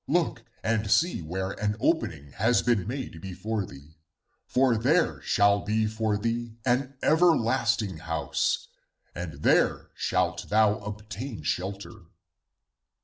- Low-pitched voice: Yes, low, 110 Hz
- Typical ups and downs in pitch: Yes, average, 3.7 semitones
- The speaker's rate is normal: No, slow, 125 wpm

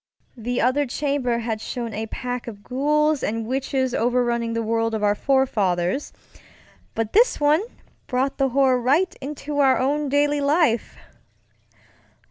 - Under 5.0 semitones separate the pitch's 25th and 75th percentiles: Yes, average, 3.8 semitones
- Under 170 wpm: Yes, average, 140 wpm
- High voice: Yes, very high, 255 Hz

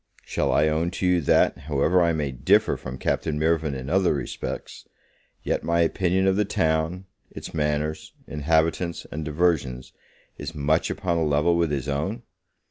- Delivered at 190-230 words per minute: No, average, 170 wpm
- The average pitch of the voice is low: Yes, very low, 80 Hz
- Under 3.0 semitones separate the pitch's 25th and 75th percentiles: Yes, narrow, 2.6 semitones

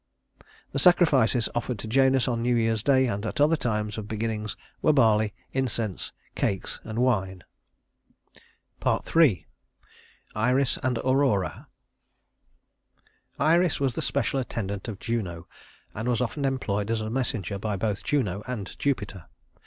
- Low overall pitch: Yes, low, 115 Hz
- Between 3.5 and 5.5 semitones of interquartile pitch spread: Yes, average, 3.9 semitones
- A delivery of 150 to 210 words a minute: No, slow, 135 wpm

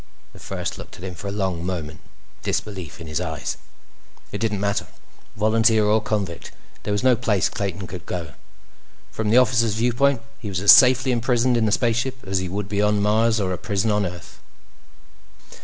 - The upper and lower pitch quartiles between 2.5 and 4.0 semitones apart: Yes, average, 3.5 semitones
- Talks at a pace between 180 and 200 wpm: Yes, average, 190 wpm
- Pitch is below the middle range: Yes, low, 105 Hz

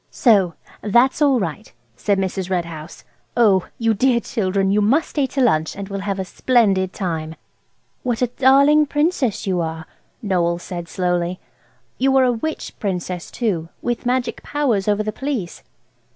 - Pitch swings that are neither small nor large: No, wide, 5.7 semitones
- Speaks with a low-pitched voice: No, high, 205 Hz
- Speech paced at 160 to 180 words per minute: Yes, average, 165 wpm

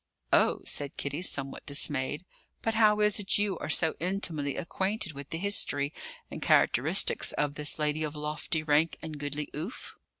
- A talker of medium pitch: Yes, medium, 155 Hz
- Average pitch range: Yes, average, 4.5 semitones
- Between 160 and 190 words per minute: Yes, average, 165 wpm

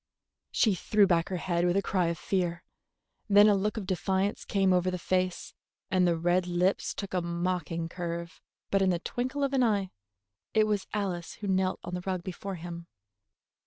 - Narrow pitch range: Yes, narrow, 2.2 semitones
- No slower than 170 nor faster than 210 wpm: Yes, average, 195 wpm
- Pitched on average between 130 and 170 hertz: No, medium, 185 Hz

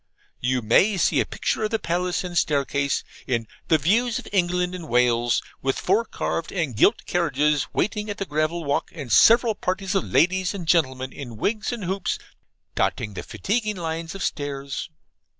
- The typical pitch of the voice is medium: Yes, medium, 170 Hz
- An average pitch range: No, wide, 5.9 semitones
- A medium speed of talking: Yes, average, 175 wpm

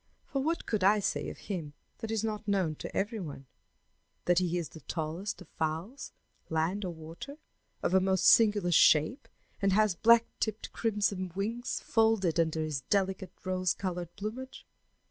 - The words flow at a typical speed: Yes, average, 165 wpm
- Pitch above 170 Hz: Yes, high, 190 Hz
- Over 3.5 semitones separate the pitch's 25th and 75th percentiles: Yes, average, 4.2 semitones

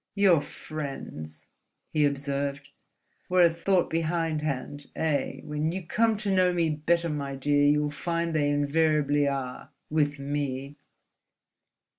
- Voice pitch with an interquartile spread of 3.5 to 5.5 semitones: No, average, 2.9 semitones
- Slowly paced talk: Yes, slow, 120 wpm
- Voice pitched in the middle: Yes, medium, 150 Hz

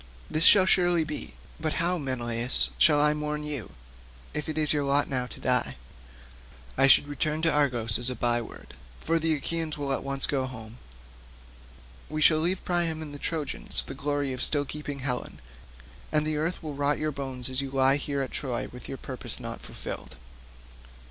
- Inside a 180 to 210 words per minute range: Yes, average, 190 wpm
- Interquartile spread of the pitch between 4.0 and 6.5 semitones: No, average, 2.9 semitones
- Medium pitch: Yes, medium, 145 Hz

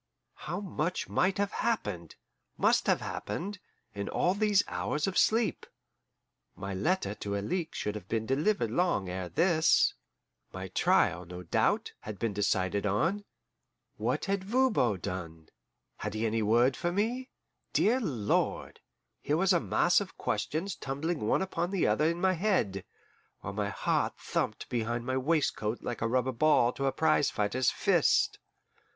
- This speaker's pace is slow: No, average, 155 wpm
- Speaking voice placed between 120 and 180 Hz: Yes, low, 135 Hz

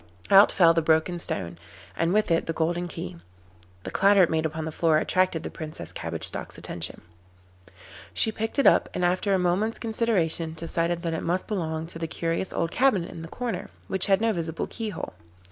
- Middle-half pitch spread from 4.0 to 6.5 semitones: No, average, 3.2 semitones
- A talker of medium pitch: Yes, medium, 170 Hz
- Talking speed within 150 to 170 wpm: No, average, 195 wpm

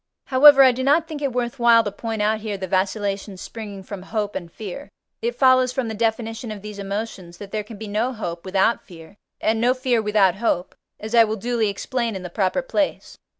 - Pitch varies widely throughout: No, average, 3.5 semitones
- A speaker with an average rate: No, fast, 220 wpm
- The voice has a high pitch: Yes, high, 220 Hz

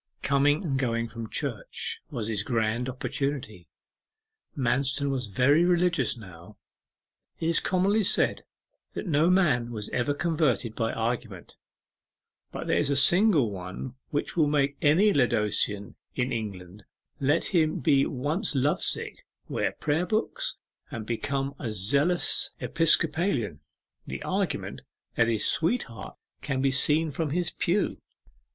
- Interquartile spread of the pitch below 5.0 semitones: No, wide, 5.6 semitones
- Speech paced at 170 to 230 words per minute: No, slow, 135 wpm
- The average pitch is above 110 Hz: Yes, low, 135 Hz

